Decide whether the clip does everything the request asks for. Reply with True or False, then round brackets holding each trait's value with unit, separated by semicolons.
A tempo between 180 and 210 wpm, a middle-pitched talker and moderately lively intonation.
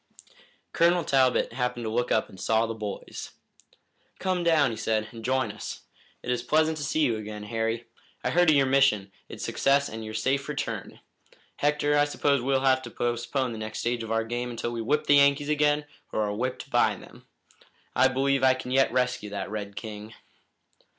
False (195 wpm; 125 Hz; 4.0 semitones)